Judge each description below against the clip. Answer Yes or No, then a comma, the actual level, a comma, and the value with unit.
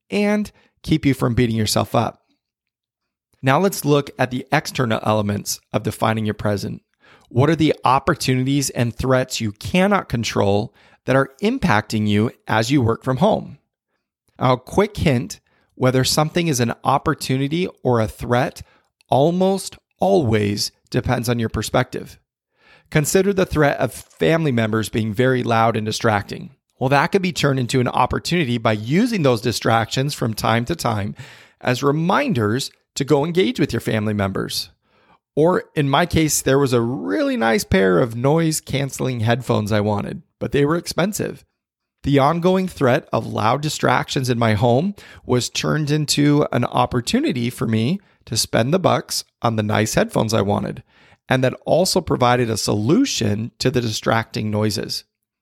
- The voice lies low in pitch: Yes, low, 125 Hz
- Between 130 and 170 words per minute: Yes, average, 160 wpm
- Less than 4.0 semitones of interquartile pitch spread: No, average, 4.7 semitones